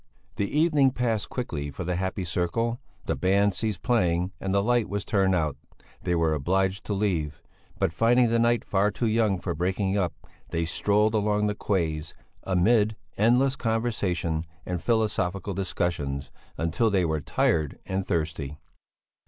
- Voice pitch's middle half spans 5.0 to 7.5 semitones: No, average, 4.3 semitones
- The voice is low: Yes, very low, 95 Hz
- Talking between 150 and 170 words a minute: Yes, average, 155 wpm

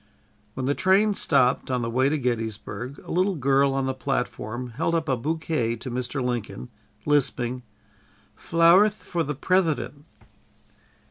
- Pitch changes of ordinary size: Yes, average, 4.6 semitones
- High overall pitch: No, low, 135 Hz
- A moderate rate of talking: Yes, average, 150 wpm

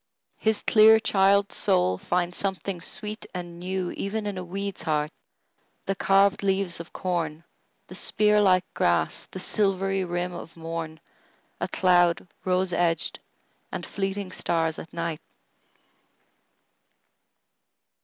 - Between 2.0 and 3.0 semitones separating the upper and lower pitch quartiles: Yes, average, 2.7 semitones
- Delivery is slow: Yes, slow, 115 wpm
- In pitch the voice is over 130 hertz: Yes, medium, 185 Hz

